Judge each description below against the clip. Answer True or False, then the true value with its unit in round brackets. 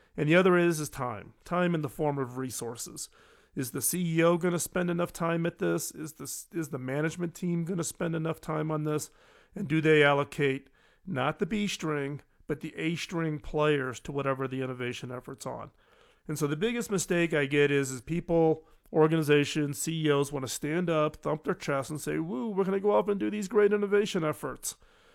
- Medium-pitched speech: True (155 Hz)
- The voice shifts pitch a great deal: False (3.7 semitones)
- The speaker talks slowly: False (200 wpm)